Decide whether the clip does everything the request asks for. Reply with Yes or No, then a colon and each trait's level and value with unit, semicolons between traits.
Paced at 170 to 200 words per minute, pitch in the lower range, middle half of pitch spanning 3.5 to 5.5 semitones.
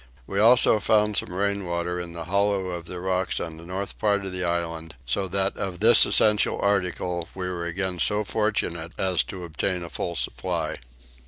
No: average, 185 wpm; very low, 90 Hz; narrow, 2.6 semitones